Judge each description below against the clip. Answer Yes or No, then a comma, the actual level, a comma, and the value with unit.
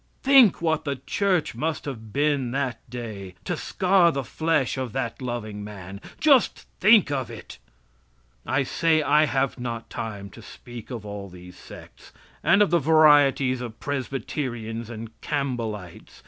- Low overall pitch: Yes, low, 130 Hz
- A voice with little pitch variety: No, average, 5.2 semitones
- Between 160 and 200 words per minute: No, average, 150 wpm